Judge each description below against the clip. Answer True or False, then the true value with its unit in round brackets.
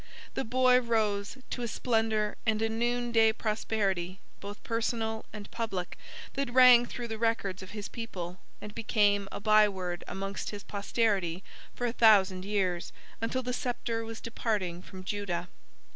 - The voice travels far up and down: False (2.8 semitones)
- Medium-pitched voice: False (215 Hz)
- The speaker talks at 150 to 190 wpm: True (155 wpm)